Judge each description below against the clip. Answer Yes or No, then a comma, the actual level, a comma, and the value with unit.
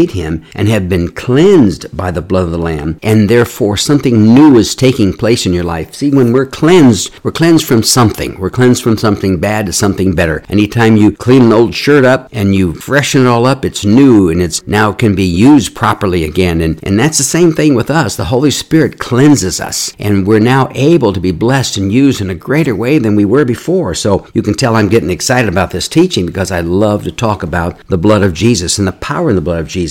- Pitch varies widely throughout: Yes, wide, 5.7 semitones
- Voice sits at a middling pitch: No, low, 105 Hz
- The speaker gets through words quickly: Yes, fast, 240 wpm